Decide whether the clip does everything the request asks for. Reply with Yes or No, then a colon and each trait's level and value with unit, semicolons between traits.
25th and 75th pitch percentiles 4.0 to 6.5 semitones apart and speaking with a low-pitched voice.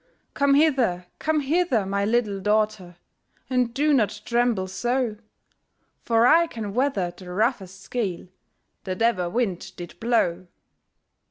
No: average, 4.7 semitones; high, 220 Hz